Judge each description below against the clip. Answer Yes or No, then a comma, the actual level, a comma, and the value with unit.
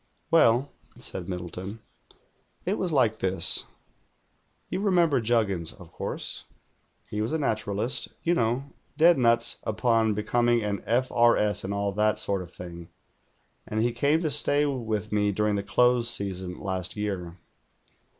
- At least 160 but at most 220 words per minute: No, average, 150 wpm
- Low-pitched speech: Yes, low, 110 Hz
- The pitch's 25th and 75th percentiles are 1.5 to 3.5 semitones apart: No, average, 3.9 semitones